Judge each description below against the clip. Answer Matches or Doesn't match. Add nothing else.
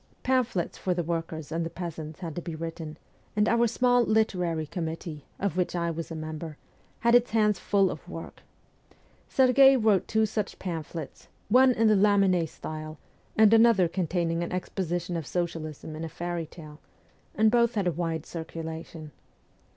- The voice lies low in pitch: Doesn't match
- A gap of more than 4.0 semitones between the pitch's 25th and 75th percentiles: Matches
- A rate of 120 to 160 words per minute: Doesn't match